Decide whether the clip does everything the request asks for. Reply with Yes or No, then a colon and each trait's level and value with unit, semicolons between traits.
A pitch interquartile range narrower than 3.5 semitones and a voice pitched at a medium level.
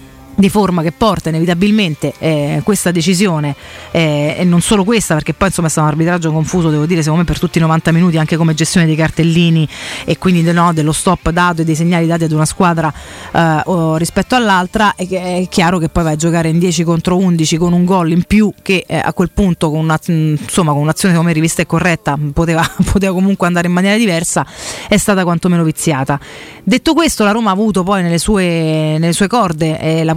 Yes: narrow, 2.6 semitones; medium, 170 Hz